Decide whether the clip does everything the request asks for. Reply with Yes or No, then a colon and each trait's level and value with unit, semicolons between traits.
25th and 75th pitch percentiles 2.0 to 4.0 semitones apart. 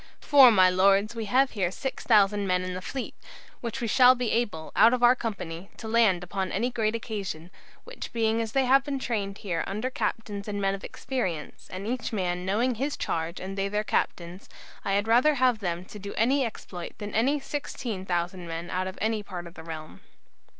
No: average, 4.4 semitones